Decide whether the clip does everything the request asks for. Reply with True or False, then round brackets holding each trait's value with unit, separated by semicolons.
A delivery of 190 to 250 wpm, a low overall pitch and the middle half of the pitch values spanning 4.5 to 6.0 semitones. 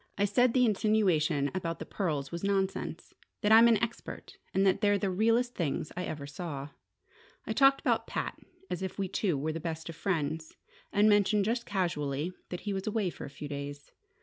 False (200 wpm; 190 Hz; 5.0 semitones)